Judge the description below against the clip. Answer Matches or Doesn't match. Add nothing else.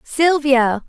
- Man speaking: Doesn't match